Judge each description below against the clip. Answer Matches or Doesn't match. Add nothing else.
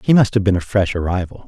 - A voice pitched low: Matches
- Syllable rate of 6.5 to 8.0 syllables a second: Matches